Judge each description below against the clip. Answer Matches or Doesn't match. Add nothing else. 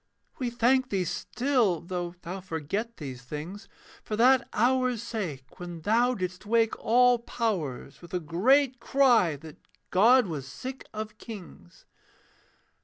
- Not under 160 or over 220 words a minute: Doesn't match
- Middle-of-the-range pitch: Doesn't match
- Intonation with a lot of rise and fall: Matches